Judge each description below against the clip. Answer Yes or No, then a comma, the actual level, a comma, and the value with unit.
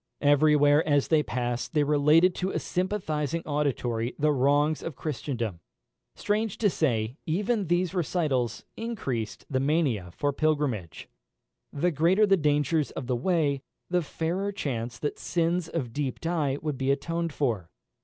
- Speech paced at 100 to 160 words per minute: Yes, average, 150 wpm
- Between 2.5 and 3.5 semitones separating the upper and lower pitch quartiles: No, average, 4.2 semitones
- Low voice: No, medium, 150 Hz